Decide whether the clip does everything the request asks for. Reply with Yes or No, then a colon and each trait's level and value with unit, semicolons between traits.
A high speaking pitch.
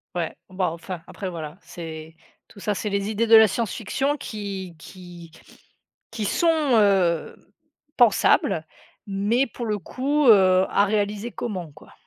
Yes: high, 200 Hz